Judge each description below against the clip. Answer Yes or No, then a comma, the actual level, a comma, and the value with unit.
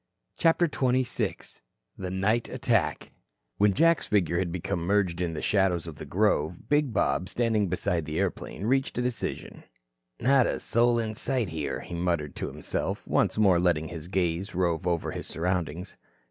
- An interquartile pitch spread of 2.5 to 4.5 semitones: No, average, 5.0 semitones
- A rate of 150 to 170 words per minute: Yes, average, 165 wpm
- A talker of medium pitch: No, very low, 95 Hz